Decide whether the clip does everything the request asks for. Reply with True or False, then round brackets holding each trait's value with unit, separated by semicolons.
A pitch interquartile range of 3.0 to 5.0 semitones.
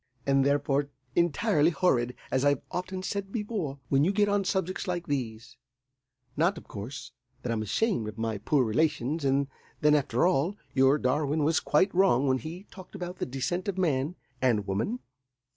False (5.6 semitones)